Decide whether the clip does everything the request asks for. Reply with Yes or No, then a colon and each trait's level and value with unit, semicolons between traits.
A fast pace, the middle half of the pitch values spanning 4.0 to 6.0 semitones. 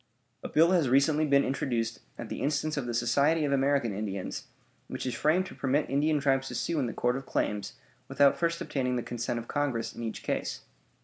No: fast, 210 wpm; average, 3.5 semitones